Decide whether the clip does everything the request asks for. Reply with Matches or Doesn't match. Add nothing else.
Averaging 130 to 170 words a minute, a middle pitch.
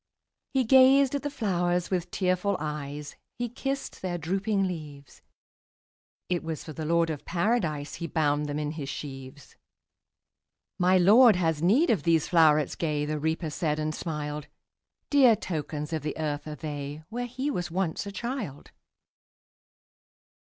Matches